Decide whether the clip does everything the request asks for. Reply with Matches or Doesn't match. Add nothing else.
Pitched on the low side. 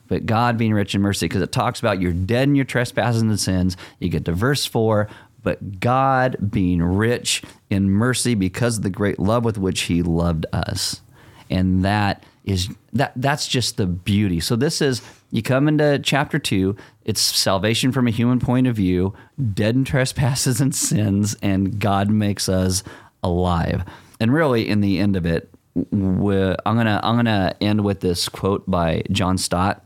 Matches